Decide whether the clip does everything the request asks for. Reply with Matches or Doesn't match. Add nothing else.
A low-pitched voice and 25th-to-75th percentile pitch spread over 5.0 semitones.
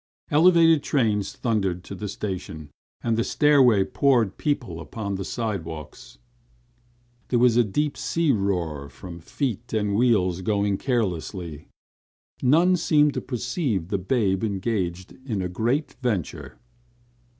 Matches